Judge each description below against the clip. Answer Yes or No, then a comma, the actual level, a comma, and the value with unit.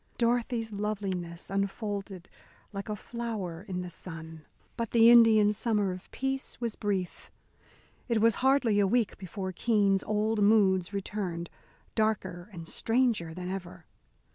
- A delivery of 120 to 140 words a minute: Yes, slow, 135 wpm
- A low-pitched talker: No, high, 205 Hz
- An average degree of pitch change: Yes, average, 3.6 semitones